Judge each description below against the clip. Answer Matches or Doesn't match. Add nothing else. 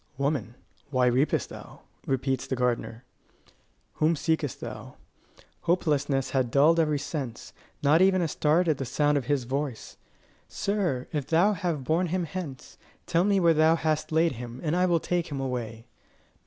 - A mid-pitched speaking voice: Matches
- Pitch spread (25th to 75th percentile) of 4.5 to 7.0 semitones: Doesn't match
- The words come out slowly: Doesn't match